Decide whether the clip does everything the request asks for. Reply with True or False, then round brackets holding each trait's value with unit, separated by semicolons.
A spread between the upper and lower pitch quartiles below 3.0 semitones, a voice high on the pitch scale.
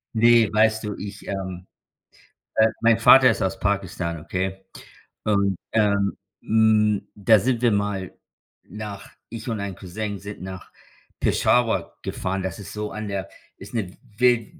False (2.4 semitones; 105 Hz)